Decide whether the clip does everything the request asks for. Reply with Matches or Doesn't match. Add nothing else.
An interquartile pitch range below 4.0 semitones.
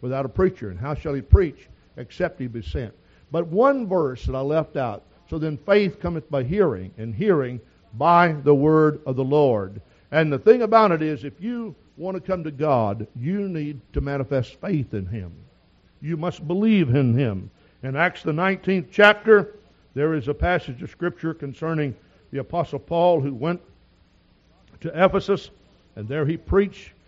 Doesn't match